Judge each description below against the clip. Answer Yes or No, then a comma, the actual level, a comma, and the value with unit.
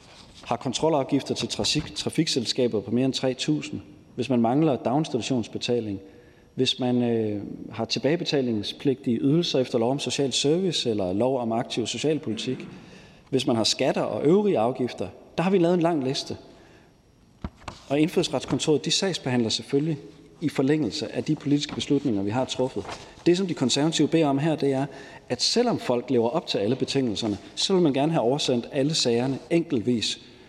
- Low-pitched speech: Yes, low, 130 Hz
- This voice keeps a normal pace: Yes, average, 165 wpm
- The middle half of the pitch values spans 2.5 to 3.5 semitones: No, average, 3.9 semitones